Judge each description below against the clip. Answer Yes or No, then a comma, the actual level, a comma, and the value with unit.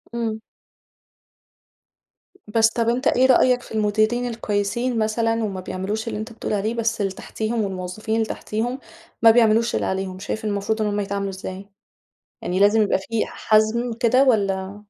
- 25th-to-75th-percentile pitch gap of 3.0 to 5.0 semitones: No, narrow, 2.4 semitones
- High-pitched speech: Yes, high, 220 Hz